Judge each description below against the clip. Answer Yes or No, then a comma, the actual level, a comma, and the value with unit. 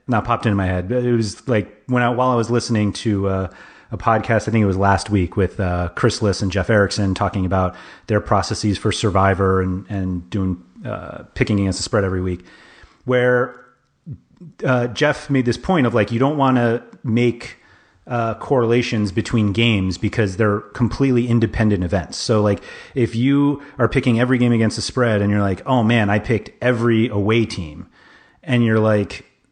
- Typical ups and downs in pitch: Yes, average, 3.4 semitones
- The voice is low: Yes, low, 110 Hz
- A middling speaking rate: Yes, average, 190 wpm